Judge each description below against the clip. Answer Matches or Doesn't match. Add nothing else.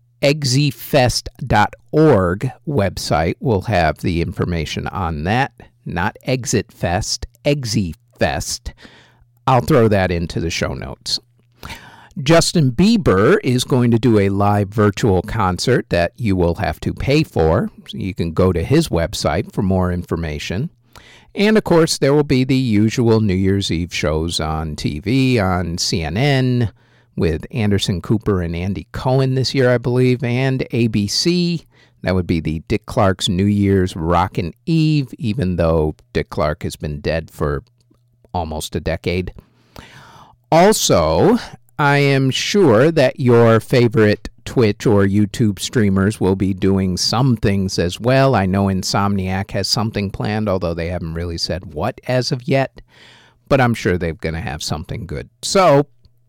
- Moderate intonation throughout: Doesn't match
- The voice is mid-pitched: Doesn't match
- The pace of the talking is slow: Doesn't match